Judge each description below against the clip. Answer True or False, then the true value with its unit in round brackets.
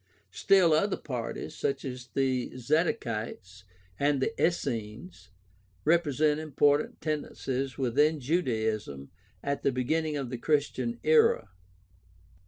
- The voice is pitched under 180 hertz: True (135 Hz)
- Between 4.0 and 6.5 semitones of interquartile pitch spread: True (4.4 semitones)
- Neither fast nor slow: False (110 wpm)